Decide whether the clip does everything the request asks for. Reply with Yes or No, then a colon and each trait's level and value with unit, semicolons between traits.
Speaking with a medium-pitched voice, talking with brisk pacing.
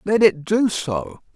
No: medium, 170 Hz; average, 175 wpm